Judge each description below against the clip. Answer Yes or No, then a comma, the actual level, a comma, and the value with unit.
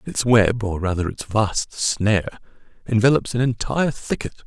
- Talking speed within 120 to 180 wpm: Yes, average, 150 wpm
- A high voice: No, low, 110 Hz